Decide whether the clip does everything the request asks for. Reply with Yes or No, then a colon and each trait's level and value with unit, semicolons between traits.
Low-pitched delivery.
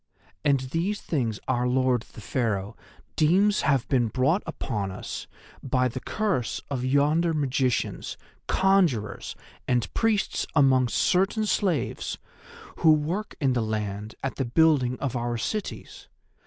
Yes: low, 130 Hz